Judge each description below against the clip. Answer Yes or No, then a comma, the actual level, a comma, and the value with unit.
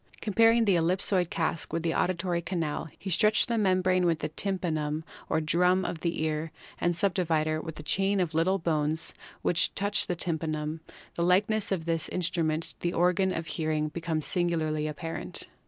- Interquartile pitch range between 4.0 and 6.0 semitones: No, average, 2.7 semitones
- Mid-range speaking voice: Yes, medium, 170 Hz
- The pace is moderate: Yes, average, 175 wpm